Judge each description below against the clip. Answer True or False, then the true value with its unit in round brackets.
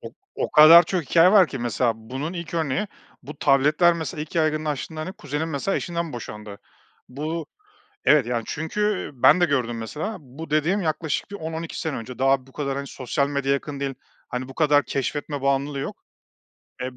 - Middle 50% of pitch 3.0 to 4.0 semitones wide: True (3.3 semitones)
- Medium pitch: True (150 Hz)